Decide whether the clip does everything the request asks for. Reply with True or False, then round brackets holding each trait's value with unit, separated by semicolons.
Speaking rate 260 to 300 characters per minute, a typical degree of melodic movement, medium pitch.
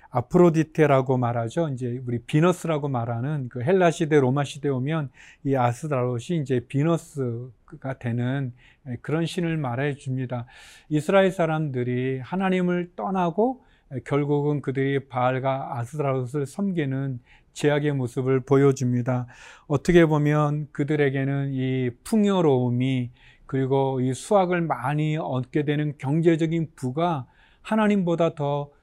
True (290 characters per minute; 4.0 semitones; 145 Hz)